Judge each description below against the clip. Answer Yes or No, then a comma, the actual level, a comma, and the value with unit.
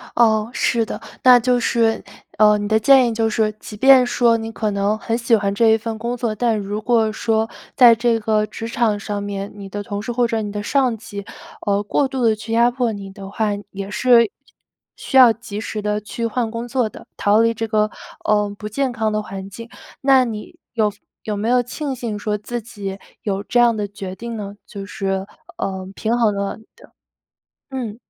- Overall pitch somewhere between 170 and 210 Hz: No, high, 220 Hz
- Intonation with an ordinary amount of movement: No, narrow, 2.3 semitones